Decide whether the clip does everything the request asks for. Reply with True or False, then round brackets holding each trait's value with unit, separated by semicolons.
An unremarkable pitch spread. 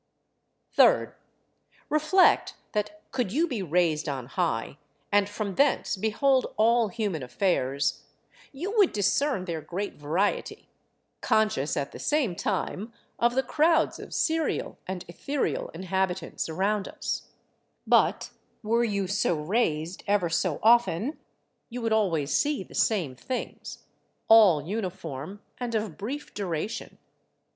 False (5.8 semitones)